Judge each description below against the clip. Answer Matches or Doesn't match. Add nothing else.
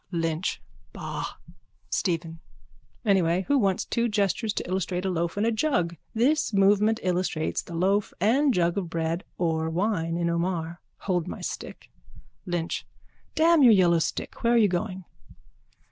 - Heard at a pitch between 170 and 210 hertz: Matches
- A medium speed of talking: Matches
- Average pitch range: Matches